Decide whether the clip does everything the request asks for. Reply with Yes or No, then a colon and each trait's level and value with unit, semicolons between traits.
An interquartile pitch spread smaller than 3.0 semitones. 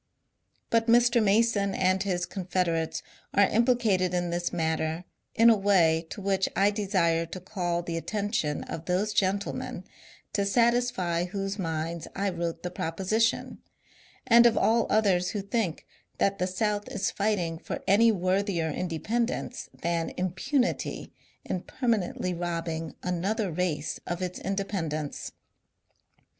No: average, 3.6 semitones